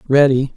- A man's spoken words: Yes, male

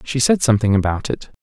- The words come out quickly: Yes, fast, 210 wpm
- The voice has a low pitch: Yes, low, 120 Hz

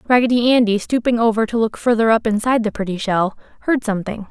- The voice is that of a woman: Yes, female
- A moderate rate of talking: Yes, average, 195 wpm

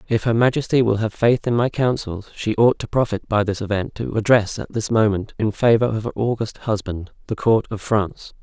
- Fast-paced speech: Yes, fast, 220 wpm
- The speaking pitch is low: Yes, low, 110 Hz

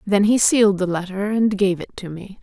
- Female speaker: Yes, female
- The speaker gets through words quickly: Yes, fast, 245 wpm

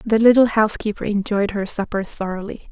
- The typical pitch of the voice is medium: No, high, 210 Hz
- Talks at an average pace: Yes, average, 155 wpm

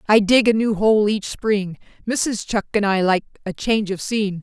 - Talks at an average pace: No, fast, 215 wpm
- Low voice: No, high, 210 Hz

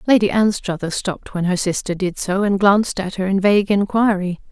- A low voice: No, high, 195 Hz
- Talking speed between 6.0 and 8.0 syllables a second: No, 5.6 syllables/s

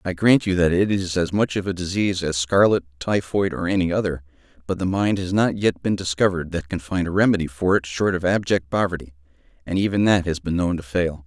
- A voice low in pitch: Yes, very low, 90 Hz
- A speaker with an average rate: No, fast, 235 wpm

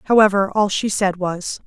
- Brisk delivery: No, average, 180 wpm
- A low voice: No, high, 195 Hz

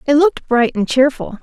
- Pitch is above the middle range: Yes, very high, 270 Hz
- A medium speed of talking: No, fast, 210 wpm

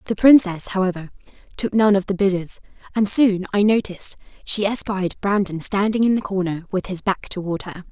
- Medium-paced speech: Yes, average, 180 wpm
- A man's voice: No, female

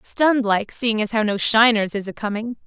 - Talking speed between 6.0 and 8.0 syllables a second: No, 5.2 syllables/s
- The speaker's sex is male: No, female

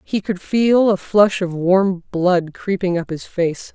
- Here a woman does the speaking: Yes, female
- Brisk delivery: No, average, 190 wpm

